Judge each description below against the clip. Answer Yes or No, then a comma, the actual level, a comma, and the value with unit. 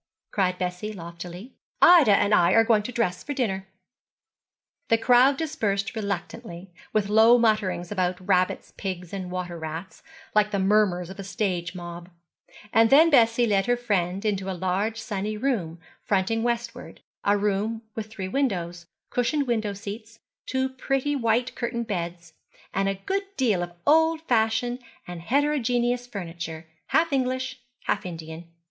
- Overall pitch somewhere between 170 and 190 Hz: No, high, 210 Hz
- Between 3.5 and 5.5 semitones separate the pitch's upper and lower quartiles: Yes, average, 4.9 semitones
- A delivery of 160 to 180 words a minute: No, average, 150 wpm